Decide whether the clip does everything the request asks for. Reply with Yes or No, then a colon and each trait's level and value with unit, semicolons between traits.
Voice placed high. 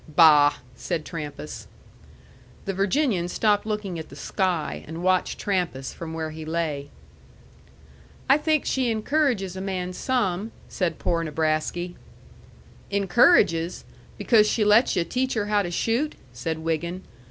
No: medium, 180 Hz